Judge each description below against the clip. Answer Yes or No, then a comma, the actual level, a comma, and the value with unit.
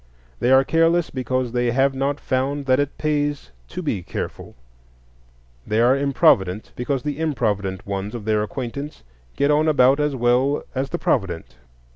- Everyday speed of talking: Yes, average, 160 wpm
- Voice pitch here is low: Yes, low, 130 Hz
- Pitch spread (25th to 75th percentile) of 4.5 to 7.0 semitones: No, average, 3.8 semitones